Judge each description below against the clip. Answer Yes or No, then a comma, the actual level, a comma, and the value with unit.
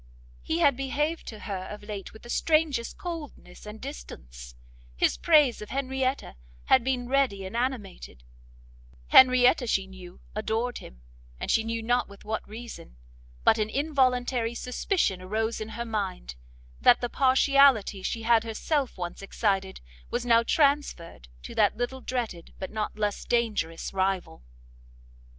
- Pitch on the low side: No, high, 230 Hz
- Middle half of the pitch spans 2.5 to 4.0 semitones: No, average, 4.9 semitones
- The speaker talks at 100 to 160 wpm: Yes, average, 145 wpm